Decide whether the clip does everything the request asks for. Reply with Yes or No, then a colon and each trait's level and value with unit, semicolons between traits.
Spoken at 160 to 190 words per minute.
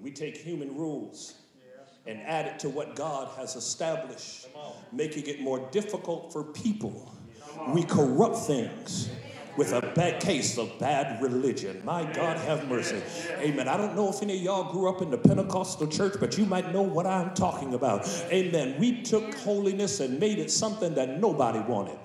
Yes: average, 175 wpm